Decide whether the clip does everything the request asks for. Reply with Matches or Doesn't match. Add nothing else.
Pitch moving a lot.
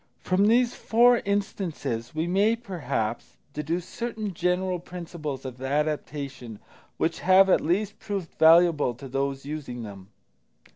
Matches